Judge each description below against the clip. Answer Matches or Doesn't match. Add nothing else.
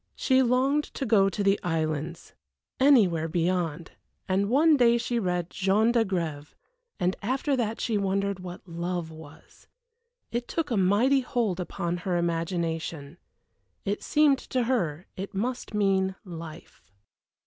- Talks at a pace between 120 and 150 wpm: Matches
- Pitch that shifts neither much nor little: Doesn't match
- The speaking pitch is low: Doesn't match